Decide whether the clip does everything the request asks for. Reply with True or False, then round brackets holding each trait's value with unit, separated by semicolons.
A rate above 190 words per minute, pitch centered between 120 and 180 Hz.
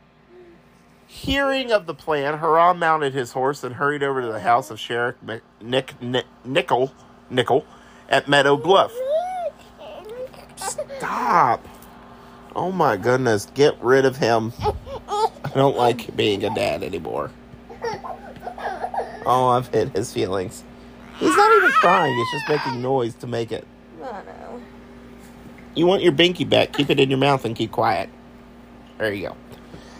False (140 wpm; 140 Hz)